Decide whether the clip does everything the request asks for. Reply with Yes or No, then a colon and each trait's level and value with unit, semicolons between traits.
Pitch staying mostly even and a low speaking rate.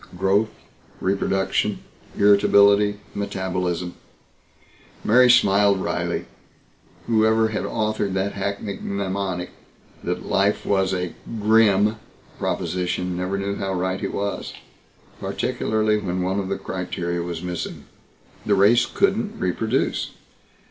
Yes: narrow, 2.2 semitones; slow, 105 wpm